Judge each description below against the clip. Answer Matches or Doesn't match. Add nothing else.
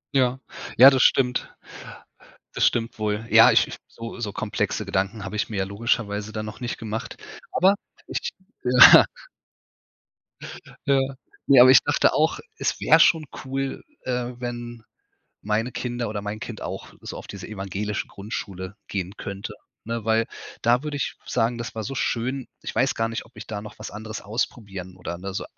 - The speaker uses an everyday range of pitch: Matches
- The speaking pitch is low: Matches